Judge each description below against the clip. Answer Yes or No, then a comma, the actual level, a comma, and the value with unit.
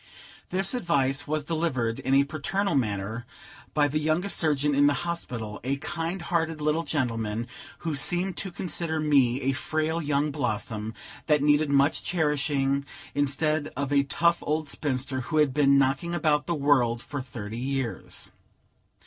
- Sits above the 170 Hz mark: No, medium, 145 Hz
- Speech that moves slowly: No, average, 155 wpm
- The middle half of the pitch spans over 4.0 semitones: No, average, 3.1 semitones